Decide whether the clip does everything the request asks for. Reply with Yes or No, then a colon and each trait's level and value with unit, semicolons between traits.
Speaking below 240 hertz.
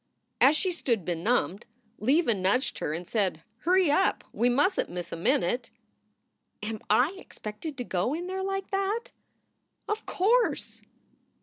No: very high, 255 Hz